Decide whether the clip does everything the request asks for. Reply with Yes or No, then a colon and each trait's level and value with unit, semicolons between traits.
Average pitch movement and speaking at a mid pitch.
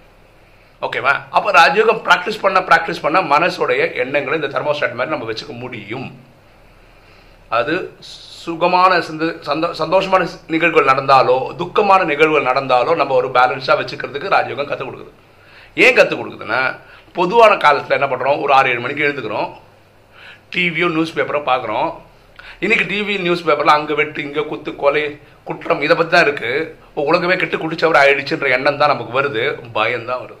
Yes: average, 4.4 semitones; medium, 160 Hz